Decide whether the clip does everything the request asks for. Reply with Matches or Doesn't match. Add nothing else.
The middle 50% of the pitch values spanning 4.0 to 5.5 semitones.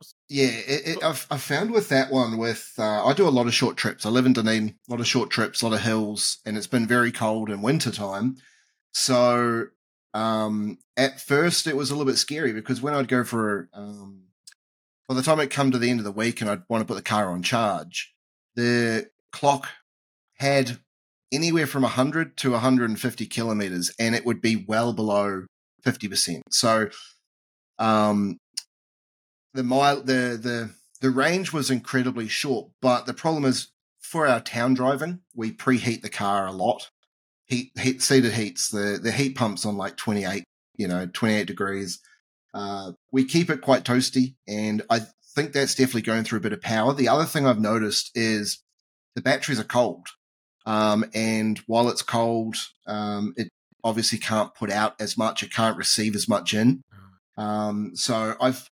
Doesn't match